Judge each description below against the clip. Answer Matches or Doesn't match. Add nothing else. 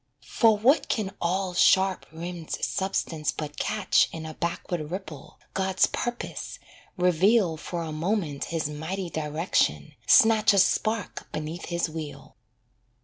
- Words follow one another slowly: Matches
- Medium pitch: Matches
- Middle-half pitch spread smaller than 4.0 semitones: Matches